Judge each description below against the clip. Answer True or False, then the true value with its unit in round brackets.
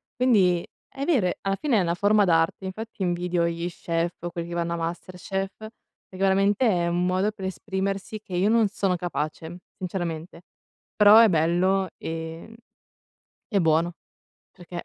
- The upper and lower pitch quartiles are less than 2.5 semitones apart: False (2.8 semitones)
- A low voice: False (185 Hz)